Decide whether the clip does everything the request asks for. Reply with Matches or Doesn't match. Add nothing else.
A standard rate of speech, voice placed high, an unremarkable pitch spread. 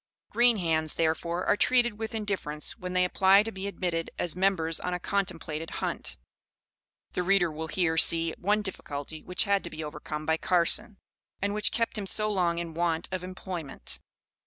Doesn't match